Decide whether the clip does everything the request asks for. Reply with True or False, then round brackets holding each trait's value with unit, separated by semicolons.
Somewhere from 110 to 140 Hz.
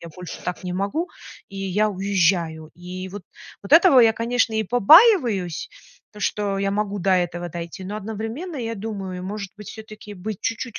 False (200 Hz)